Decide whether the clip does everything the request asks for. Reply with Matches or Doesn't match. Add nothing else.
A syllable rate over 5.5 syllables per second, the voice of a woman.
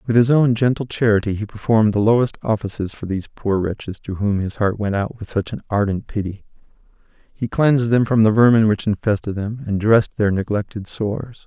Doesn't match